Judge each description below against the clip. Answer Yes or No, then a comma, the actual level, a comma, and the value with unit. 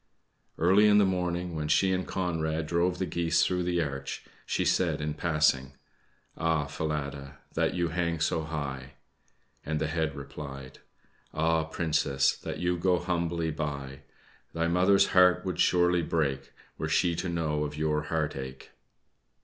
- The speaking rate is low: No, average, 155 wpm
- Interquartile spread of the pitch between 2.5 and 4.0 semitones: Yes, average, 2.9 semitones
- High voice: No, very low, 80 Hz